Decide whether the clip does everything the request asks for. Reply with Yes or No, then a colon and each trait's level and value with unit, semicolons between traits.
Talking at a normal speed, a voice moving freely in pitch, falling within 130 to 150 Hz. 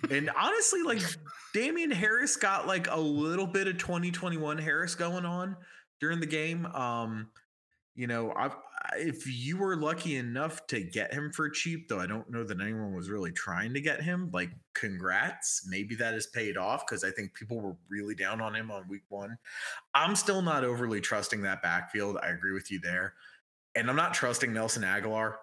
Yes: average, 190 wpm; wide, 7.7 semitones; medium, 140 Hz